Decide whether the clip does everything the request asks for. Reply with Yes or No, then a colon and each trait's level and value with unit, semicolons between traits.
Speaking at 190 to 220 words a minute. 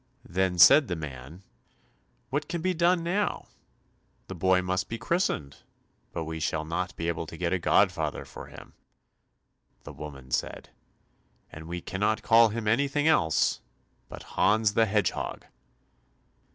No: average, 145 wpm